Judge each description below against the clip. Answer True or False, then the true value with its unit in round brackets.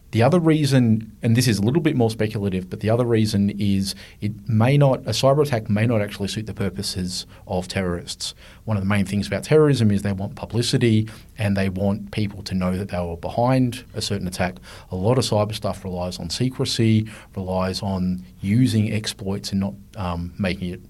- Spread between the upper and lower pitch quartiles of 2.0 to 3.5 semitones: True (2.8 semitones)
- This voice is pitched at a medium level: False (105 Hz)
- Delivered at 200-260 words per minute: True (205 wpm)